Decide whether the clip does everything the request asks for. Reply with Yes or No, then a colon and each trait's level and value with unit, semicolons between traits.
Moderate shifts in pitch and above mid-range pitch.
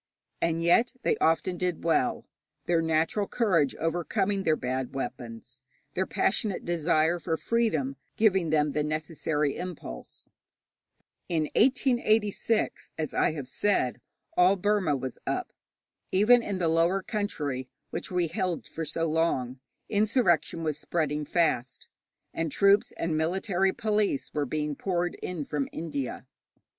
No: average, 4.4 semitones; medium, 165 Hz